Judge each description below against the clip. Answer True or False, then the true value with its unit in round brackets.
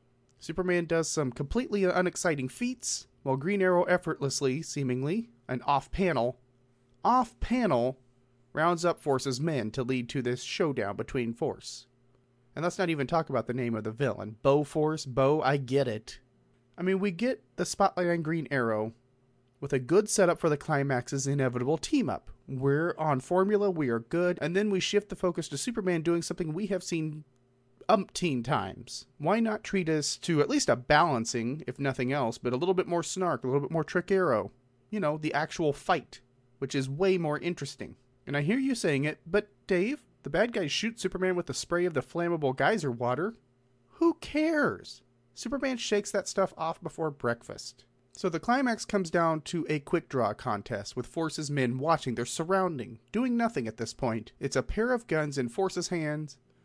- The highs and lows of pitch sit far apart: True (6.3 semitones)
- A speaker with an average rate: True (185 wpm)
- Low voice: False (150 Hz)